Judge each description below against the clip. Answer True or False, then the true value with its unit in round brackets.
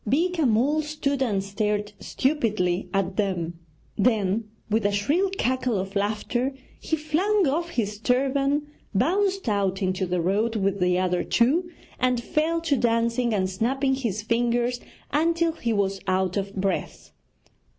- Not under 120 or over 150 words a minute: True (145 wpm)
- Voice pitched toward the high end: True (230 Hz)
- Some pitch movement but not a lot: False (6.1 semitones)